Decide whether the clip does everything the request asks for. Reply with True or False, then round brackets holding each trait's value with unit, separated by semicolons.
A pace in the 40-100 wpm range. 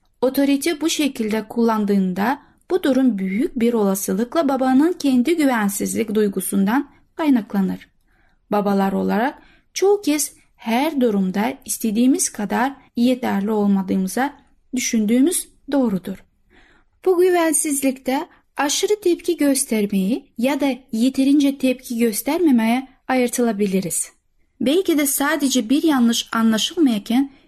True (95 wpm)